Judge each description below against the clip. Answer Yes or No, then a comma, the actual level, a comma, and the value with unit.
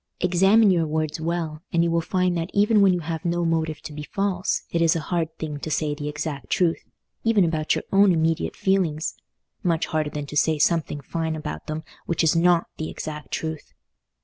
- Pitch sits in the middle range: Yes, medium, 165 Hz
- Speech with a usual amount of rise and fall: No, narrow, 2.2 semitones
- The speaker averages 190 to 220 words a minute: Yes, fast, 205 wpm